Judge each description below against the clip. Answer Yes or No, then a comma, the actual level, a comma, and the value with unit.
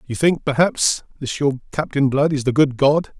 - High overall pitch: No, medium, 140 Hz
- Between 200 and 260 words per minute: Yes, fast, 205 wpm